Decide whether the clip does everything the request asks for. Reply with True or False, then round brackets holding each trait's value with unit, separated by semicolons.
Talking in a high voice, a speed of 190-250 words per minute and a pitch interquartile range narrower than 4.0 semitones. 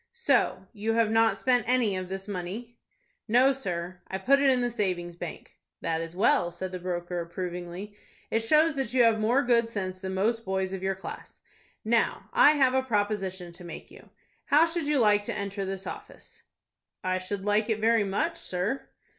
False (205 Hz; 195 wpm; 4.4 semitones)